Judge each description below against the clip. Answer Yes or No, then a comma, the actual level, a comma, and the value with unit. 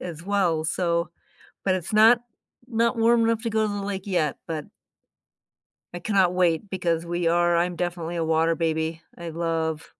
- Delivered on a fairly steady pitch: No, average, 3.3 semitones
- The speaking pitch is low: No, medium, 175 Hz